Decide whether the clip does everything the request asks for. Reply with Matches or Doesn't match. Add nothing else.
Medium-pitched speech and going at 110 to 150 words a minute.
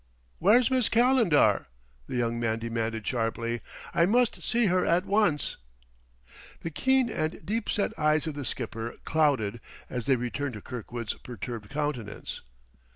Matches